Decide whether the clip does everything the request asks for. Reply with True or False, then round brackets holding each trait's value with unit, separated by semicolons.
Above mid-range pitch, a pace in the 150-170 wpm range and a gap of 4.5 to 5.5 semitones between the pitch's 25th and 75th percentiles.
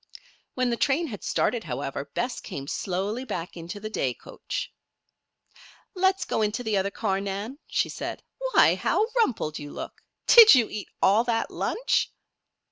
True (215 Hz; 160 wpm; 5.1 semitones)